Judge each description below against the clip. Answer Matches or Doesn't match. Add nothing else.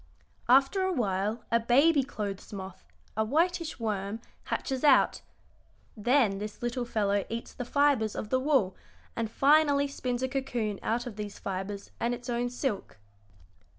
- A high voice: Matches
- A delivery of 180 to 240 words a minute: Doesn't match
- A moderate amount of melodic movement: Matches